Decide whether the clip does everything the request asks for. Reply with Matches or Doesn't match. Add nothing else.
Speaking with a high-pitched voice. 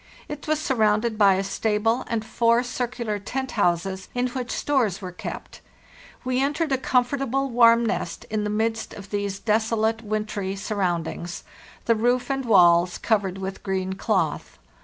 Matches